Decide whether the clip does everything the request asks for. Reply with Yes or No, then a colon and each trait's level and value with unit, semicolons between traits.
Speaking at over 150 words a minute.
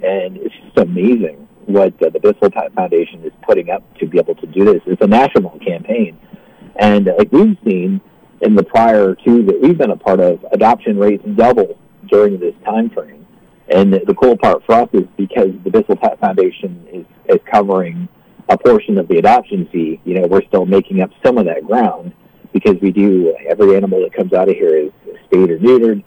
Yes: fast, 205 wpm